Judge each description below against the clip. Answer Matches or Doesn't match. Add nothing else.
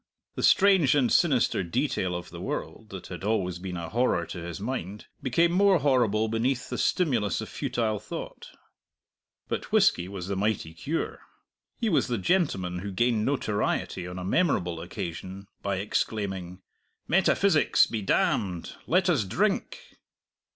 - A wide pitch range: Matches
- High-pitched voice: Doesn't match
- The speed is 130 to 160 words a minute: Matches